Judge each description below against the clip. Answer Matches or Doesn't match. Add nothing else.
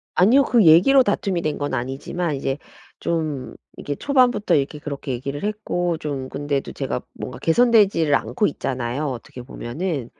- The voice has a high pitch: Doesn't match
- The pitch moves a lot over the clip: Matches